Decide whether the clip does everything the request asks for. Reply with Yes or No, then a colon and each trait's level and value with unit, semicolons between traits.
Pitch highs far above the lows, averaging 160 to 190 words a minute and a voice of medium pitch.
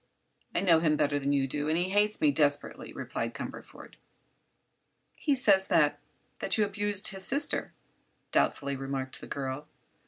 No: wide, 6.3 semitones; average, 150 wpm; medium, 155 Hz